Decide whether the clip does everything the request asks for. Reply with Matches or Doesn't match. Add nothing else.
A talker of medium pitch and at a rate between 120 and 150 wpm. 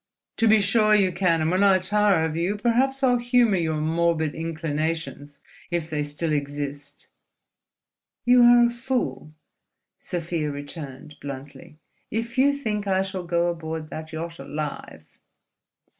Matches